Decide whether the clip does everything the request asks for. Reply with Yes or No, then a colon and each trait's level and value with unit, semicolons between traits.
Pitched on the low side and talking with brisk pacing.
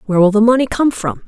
No: high, 225 Hz; fast, 280 wpm